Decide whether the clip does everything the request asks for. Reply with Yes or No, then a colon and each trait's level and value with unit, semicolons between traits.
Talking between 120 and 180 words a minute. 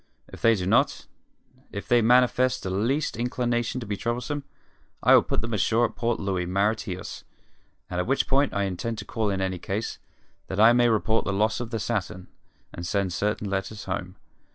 No: average, 190 wpm